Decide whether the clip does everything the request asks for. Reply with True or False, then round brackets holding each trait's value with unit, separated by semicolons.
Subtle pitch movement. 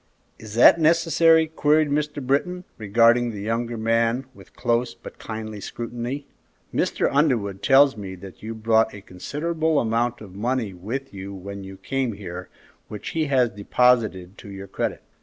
False (5.1 semitones)